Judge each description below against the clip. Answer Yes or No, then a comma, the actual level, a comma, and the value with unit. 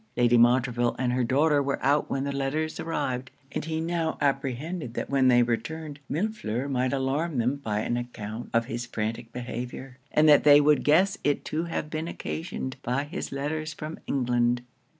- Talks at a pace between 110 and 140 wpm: No, average, 180 wpm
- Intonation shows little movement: No, average, 3.9 semitones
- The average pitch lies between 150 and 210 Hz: No, low, 135 Hz